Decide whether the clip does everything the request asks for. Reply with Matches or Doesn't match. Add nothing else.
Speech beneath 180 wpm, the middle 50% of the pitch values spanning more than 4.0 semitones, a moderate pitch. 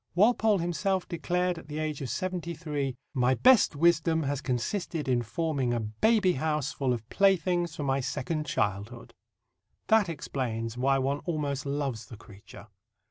Matches